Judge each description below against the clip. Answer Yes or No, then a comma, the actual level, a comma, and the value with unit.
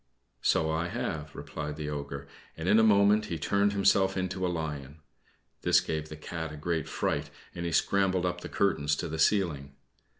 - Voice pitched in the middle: No, very low, 80 Hz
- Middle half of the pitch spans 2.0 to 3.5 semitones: No, average, 4.0 semitones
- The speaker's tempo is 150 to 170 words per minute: No, average, 190 wpm